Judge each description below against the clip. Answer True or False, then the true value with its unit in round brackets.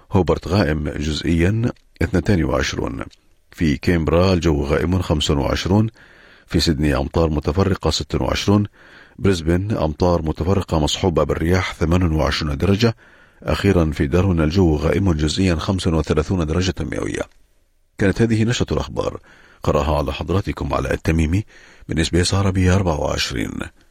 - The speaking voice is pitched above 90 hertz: False (85 Hz)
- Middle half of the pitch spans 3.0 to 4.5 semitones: True (3.5 semitones)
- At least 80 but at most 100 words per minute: False (110 wpm)